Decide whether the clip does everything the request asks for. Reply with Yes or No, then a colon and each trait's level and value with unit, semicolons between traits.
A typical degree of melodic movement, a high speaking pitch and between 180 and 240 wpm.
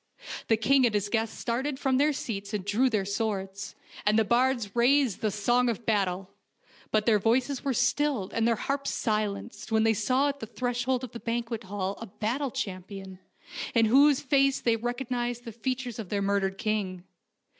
Yes: average, 3.7 semitones; high, 230 Hz; average, 185 wpm